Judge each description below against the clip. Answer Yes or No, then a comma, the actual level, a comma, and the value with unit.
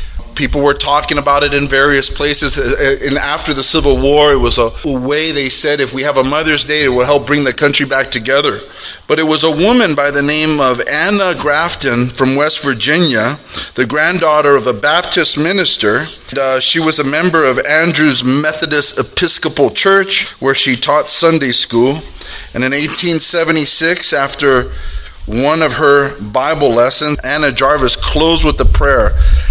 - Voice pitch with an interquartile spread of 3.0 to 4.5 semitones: No, narrow, 2.6 semitones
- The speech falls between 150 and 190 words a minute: Yes, average, 170 wpm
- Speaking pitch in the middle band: Yes, medium, 145 Hz